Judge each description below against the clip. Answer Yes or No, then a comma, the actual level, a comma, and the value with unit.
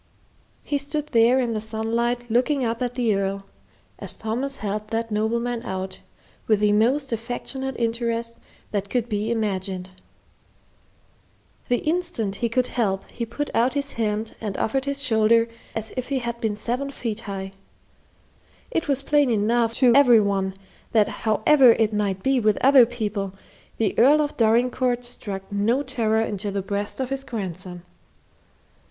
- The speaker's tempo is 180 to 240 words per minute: No, average, 160 wpm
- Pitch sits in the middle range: No, high, 230 Hz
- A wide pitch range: No, average, 3.3 semitones